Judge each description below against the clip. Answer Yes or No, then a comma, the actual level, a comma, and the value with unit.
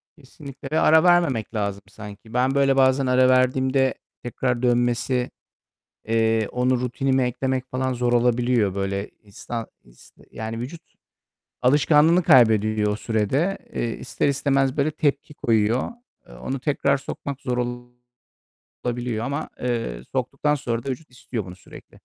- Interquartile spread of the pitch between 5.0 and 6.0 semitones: No, average, 3.1 semitones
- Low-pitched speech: Yes, low, 125 Hz